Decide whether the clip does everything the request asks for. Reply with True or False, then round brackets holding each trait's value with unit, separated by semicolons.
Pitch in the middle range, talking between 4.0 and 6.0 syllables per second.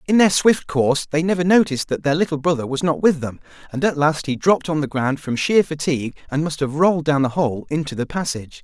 False (150 Hz; 6.2 syllables/s)